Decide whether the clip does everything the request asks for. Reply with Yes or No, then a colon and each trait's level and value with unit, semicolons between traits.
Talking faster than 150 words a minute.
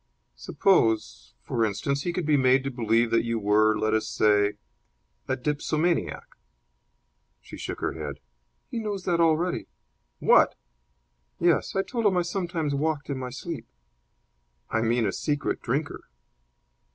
No: average, 145 wpm